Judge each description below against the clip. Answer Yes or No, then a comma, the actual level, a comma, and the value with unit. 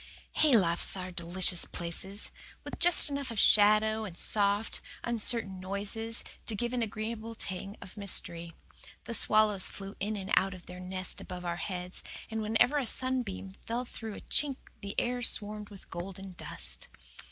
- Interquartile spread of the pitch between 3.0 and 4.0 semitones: Yes, average, 3.3 semitones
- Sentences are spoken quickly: No, average, 160 wpm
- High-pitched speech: Yes, high, 205 Hz